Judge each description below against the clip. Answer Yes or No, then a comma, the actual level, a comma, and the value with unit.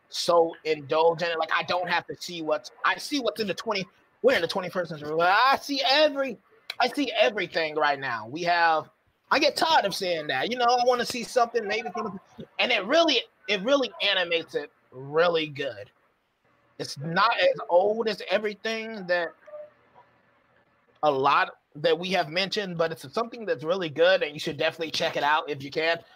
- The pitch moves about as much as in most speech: No, wide, 7.0 semitones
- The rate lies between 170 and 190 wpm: Yes, average, 185 wpm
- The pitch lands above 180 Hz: Yes, high, 190 Hz